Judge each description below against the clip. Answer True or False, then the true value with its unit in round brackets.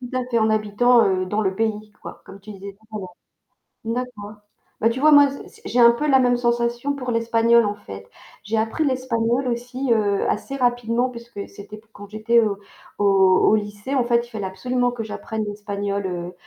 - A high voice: True (230 Hz)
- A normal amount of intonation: True (3.0 semitones)